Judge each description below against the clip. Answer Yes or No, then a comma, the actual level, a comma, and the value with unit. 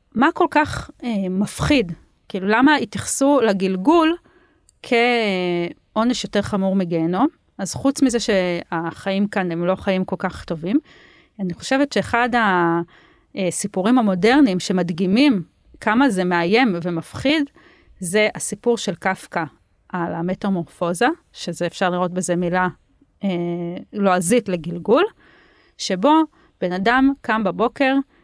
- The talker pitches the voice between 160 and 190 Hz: No, high, 200 Hz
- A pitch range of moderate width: No, wide, 5.8 semitones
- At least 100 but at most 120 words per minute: Yes, average, 115 wpm